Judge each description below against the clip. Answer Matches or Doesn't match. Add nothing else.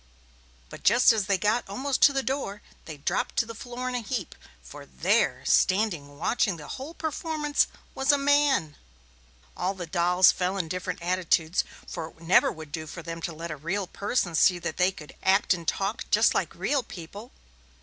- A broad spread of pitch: Matches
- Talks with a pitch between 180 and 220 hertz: Matches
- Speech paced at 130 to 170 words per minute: Doesn't match